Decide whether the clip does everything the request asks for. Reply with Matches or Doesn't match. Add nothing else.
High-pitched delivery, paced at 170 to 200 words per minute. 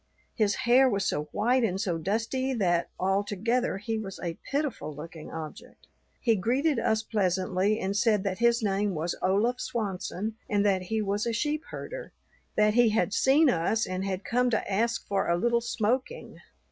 Matches